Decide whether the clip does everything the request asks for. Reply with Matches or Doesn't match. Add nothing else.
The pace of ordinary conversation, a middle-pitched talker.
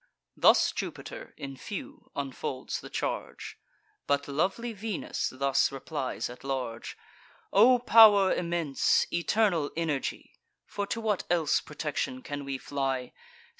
Doesn't match